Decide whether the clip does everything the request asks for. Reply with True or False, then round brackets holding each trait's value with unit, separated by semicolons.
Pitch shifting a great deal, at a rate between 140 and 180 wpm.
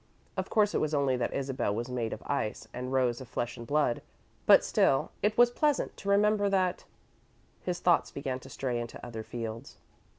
False (7.5 semitones; 195 wpm)